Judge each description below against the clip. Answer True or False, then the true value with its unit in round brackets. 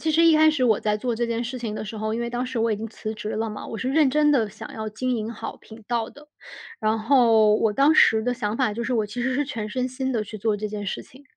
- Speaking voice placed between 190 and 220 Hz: False (230 Hz)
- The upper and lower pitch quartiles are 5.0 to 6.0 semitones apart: False (3.1 semitones)